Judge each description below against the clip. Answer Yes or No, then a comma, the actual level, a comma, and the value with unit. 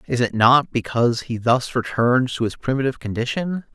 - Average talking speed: Yes, average, 175 wpm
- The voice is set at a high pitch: No, low, 125 Hz